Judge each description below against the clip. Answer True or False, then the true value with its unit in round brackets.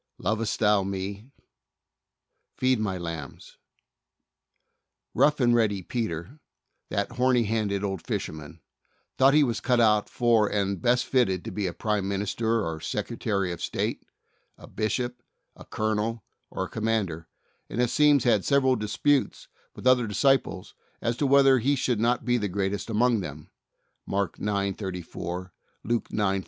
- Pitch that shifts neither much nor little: True (4.0 semitones)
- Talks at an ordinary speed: True (155 wpm)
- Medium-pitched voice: False (110 Hz)